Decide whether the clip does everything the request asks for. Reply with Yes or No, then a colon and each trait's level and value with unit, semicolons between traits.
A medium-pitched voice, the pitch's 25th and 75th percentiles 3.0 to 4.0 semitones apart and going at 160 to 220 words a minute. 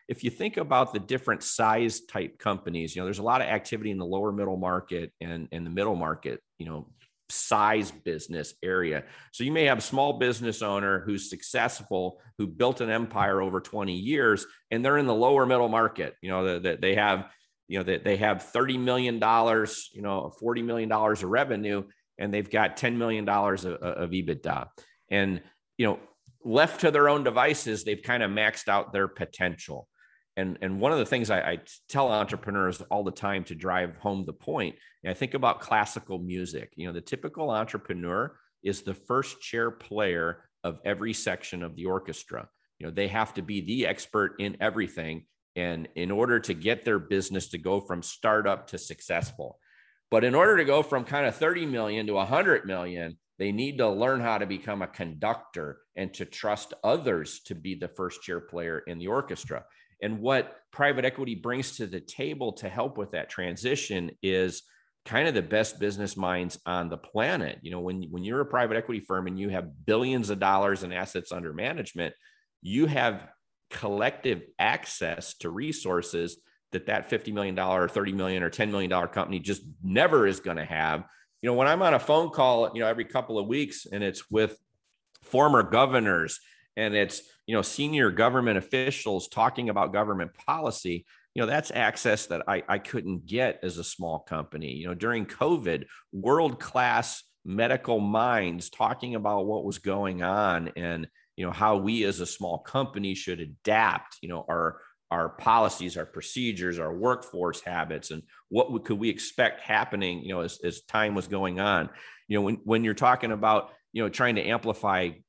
No: low, 100 Hz; average, 3.7 semitones; average, 190 wpm